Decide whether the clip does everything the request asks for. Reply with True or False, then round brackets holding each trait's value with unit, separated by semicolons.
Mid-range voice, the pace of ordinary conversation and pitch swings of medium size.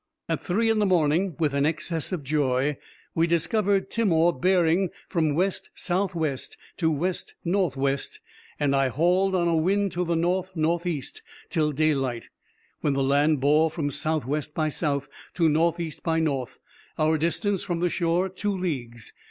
True (165 Hz; 175 wpm; 3.5 semitones)